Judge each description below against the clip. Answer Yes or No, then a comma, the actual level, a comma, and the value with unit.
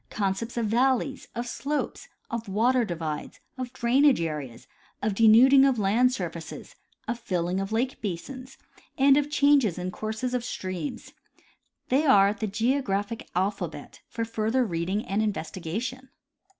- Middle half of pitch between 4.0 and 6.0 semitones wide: Yes, average, 4.9 semitones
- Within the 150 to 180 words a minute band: No, average, 140 wpm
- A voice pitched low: No, high, 225 Hz